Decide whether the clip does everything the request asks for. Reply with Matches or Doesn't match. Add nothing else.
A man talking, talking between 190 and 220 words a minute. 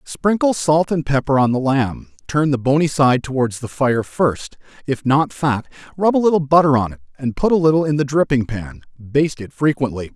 Matches